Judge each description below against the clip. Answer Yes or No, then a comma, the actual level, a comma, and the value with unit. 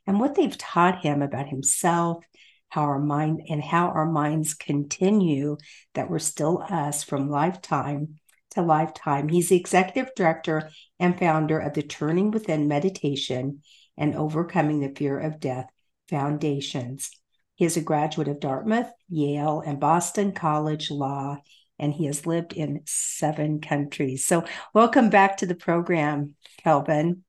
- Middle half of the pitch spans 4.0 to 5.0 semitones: No, average, 3.0 semitones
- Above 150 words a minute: No, average, 145 wpm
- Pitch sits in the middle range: Yes, medium, 155 Hz